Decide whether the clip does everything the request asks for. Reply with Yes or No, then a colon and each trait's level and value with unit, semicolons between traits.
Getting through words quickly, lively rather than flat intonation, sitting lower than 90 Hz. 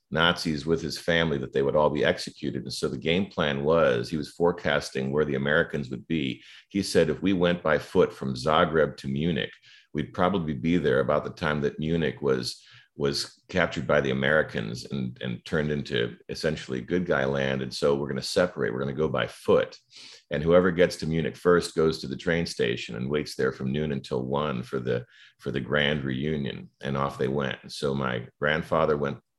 No: fast, 210 wpm; average, 3.3 semitones; very low, 75 Hz